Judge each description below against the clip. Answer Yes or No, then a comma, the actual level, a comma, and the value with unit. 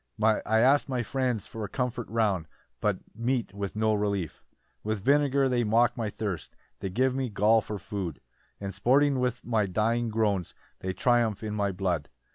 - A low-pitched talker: Yes, low, 110 Hz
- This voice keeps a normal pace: Yes, average, 175 wpm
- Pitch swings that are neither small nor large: Yes, average, 3.4 semitones